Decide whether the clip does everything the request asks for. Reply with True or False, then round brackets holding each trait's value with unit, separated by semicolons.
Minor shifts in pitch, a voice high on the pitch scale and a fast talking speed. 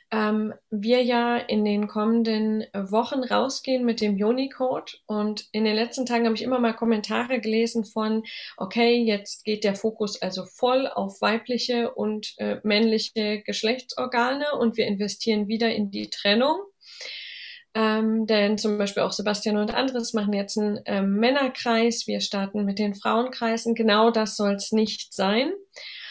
False (2.2 semitones; 220 Hz; 155 wpm)